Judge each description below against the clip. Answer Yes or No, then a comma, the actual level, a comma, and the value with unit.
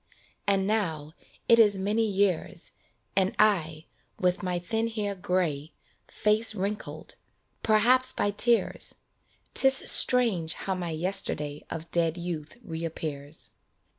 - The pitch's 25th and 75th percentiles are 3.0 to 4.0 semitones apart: No, average, 4.7 semitones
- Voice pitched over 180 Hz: Yes, high, 190 Hz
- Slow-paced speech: Yes, slow, 115 wpm